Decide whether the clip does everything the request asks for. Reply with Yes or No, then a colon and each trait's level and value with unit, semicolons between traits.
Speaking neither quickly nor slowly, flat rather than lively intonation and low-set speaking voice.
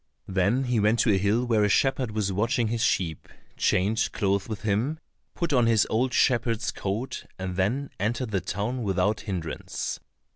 No: average, 175 wpm; average, 3.6 semitones; low, 110 Hz